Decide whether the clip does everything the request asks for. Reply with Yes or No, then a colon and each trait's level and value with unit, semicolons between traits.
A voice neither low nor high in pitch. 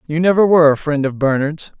Yes: medium, 155 Hz